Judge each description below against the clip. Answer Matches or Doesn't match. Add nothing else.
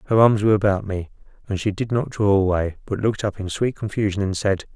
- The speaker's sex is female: Doesn't match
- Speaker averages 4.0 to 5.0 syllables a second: Doesn't match